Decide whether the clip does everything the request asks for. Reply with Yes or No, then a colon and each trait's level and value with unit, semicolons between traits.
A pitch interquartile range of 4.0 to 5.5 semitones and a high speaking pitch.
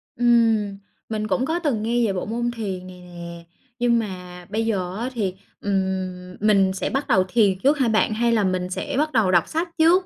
Yes: average, 4.4 semitones; high, 215 Hz